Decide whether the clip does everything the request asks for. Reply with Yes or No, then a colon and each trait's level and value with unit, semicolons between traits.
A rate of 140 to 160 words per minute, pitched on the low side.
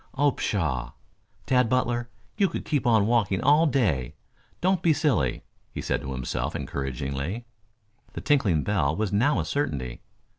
Yes: average, 150 wpm; low, 110 Hz